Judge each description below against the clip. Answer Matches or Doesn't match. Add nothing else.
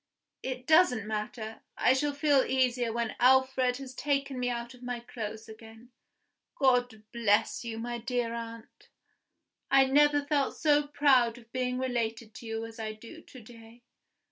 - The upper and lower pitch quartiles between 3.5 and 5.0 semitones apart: Doesn't match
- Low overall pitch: Doesn't match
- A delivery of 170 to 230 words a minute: Doesn't match